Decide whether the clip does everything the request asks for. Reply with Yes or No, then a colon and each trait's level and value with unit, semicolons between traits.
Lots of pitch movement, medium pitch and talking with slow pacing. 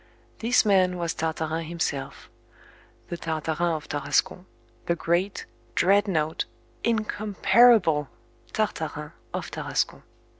No: average, 4.1 semitones; medium, 170 Hz; slow, 90 wpm